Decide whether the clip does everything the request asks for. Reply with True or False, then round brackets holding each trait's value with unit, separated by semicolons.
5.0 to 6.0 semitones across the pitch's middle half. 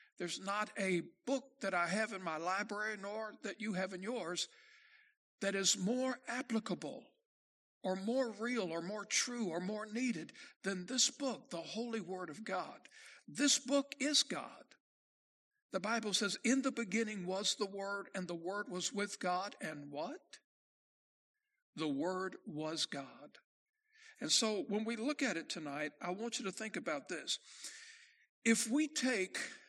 True (5.6 semitones)